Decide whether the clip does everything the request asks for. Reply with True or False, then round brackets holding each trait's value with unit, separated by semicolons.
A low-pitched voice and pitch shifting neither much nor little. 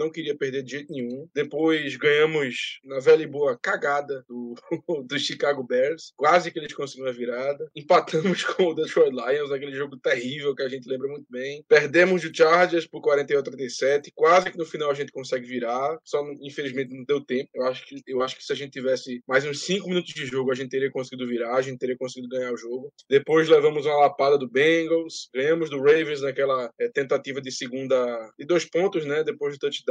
False (145 Hz; 3.9 semitones)